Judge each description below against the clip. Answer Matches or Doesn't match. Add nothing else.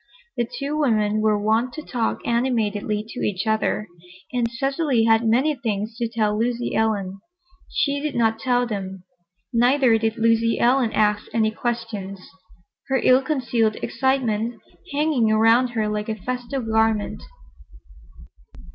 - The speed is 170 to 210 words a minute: Doesn't match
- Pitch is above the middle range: Matches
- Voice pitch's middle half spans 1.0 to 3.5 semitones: Matches